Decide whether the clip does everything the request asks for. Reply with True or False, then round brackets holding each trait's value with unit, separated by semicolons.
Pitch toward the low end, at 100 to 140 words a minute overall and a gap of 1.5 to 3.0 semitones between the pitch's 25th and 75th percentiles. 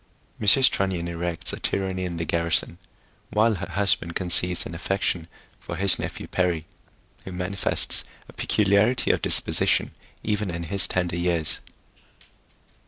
True (90 Hz; 135 wpm; 2.6 semitones)